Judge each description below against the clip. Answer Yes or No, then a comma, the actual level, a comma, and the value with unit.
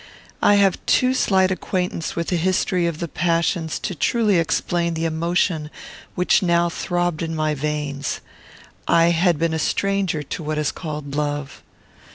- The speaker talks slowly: No, average, 160 wpm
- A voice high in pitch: No, medium, 170 Hz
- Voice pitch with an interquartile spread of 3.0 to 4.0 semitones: No, narrow, 2.6 semitones